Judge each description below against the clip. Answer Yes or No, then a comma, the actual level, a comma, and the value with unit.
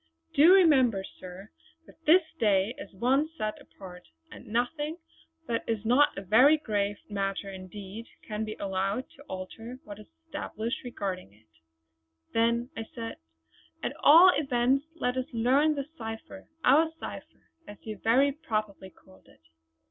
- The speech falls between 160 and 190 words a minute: No, average, 150 wpm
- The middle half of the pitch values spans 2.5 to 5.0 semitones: No, wide, 5.5 semitones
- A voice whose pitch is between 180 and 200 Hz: No, high, 225 Hz